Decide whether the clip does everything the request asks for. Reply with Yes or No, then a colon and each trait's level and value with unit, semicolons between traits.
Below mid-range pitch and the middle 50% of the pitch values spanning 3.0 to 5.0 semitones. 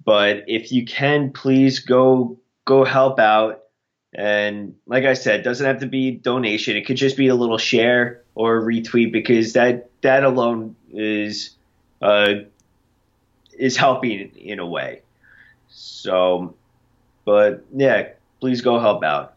Yes: low, 120 Hz; average, 3.3 semitones